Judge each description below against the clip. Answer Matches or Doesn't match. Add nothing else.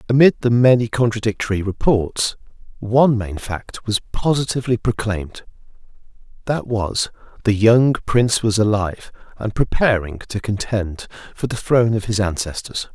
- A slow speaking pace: Matches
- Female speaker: Doesn't match